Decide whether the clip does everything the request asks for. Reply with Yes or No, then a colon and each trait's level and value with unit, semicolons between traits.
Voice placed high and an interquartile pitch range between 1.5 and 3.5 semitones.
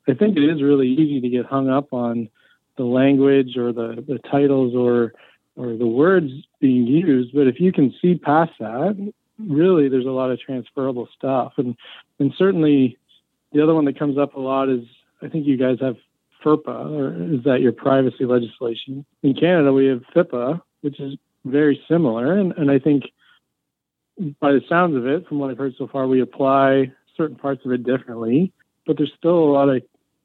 No: low, 135 Hz; average, 2.7 semitones